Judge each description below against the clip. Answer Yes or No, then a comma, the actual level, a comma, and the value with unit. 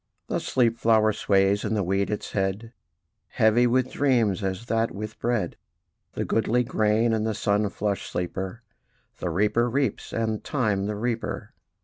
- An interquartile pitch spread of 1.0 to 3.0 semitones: Yes, average, 2.7 semitones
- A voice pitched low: Yes, low, 110 Hz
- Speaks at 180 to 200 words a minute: No, average, 155 wpm